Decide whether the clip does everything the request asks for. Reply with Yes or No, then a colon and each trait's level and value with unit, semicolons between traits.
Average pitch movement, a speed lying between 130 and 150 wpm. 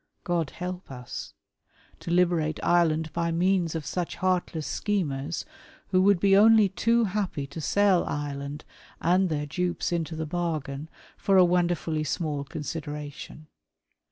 Yes: average, 3.4 semitones; slow, 135 wpm